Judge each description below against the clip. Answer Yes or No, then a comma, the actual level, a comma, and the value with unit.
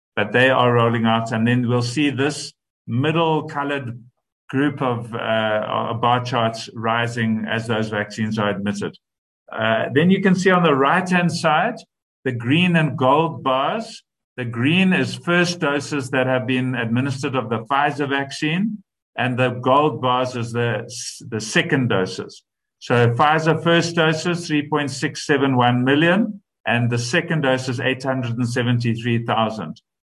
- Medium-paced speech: Yes, average, 145 wpm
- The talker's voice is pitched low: Yes, low, 130 Hz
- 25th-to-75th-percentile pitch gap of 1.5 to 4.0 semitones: No, average, 4.4 semitones